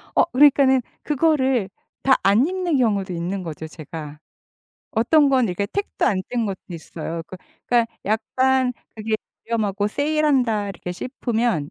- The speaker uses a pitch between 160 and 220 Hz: No, high, 230 Hz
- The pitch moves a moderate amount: No, wide, 5.8 semitones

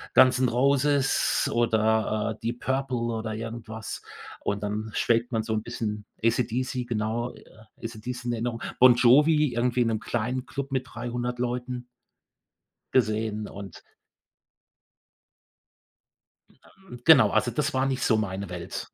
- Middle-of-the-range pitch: No, low, 120 Hz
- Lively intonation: No, narrow, 2.5 semitones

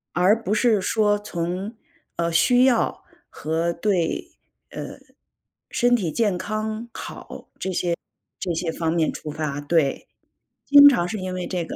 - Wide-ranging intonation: No, average, 4.3 semitones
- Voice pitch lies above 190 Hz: No, medium, 185 Hz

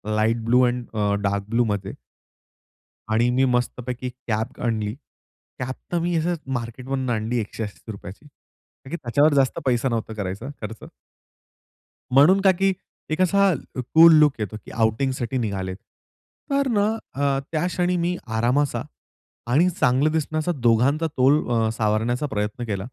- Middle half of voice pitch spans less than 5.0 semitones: No, wide, 5.4 semitones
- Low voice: Yes, low, 125 Hz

